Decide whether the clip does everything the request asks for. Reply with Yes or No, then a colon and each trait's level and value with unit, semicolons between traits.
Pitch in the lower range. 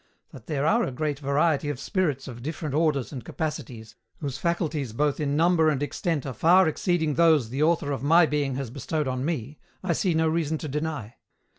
No: medium, 150 Hz